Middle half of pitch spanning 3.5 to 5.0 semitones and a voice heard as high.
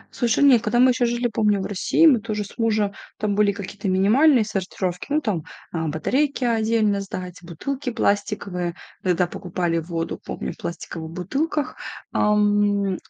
Yes: average, 4.5 semitones; high, 205 Hz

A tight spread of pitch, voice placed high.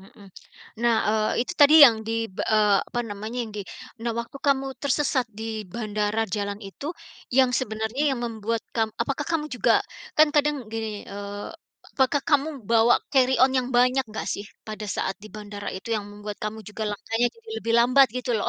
No: average, 3.7 semitones; high, 230 Hz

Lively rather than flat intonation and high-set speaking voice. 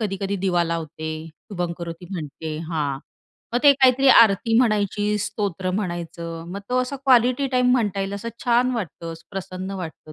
Yes: wide, 5.8 semitones; high, 195 Hz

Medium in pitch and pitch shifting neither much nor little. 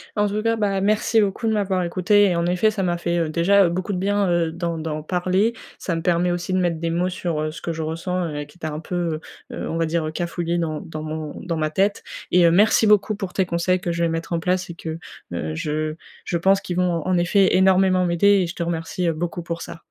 No: medium, 175 Hz; narrow, 2.3 semitones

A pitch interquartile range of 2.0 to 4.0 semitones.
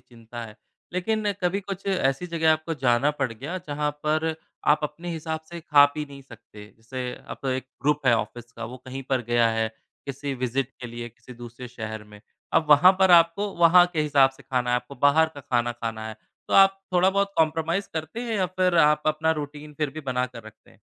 No: average, 5.1 semitones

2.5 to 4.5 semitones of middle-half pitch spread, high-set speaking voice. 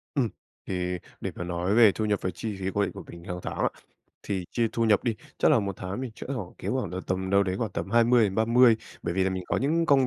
No: average, 4.1 semitones; low, 105 Hz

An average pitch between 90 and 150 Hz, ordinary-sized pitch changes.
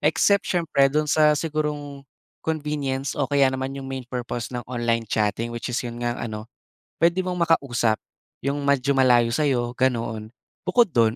Yes: low, 135 Hz; average, 4.0 semitones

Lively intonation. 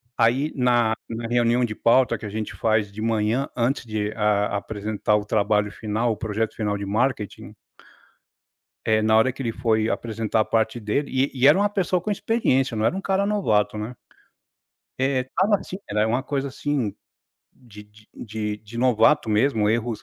No: average, 3.5 semitones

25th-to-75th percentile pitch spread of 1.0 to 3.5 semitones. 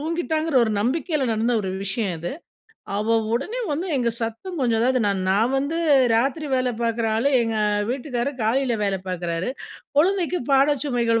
No: average, 4.5 semitones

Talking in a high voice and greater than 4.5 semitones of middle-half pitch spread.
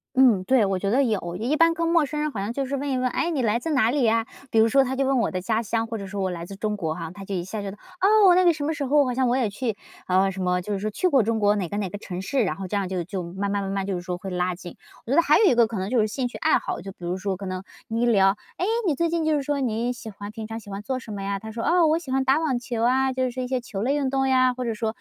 Yes: high, 225 Hz; average, 5.3 semitones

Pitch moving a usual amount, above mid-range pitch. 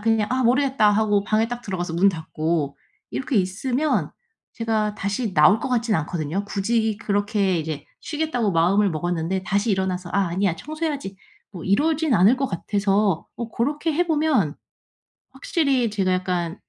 Yes: average, 5.0 semitones; high, 205 Hz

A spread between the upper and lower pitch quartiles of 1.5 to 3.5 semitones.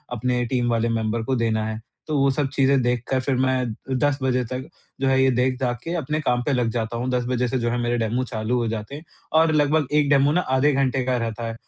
Yes: narrow, 2.5 semitones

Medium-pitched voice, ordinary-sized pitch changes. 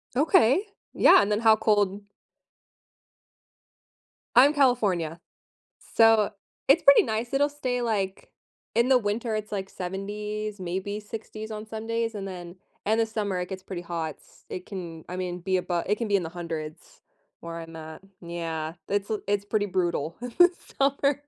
No: high, 205 Hz; average, 4.0 semitones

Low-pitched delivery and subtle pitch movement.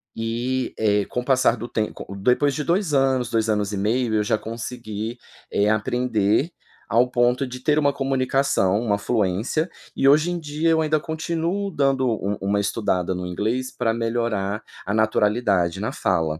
No: low, 120 Hz; average, 4.5 semitones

